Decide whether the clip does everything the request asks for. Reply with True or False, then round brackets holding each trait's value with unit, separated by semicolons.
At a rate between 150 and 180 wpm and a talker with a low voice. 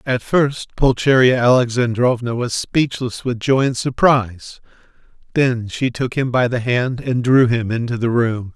True (160 wpm; 125 Hz)